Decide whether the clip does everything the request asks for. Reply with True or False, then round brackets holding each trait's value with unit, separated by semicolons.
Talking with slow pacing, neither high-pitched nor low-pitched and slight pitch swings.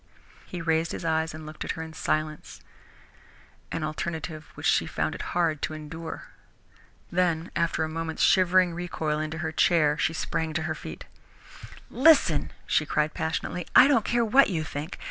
False (170 wpm; 160 Hz; 1.9 semitones)